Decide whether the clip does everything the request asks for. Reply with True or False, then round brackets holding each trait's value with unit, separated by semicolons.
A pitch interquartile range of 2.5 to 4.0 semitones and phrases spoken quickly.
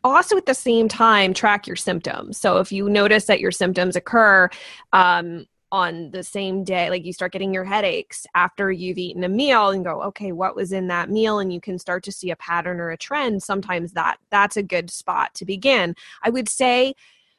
True (3.6 semitones; 215 wpm)